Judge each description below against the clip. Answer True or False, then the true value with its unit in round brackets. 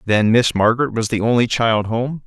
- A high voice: False (115 Hz)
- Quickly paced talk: True (210 wpm)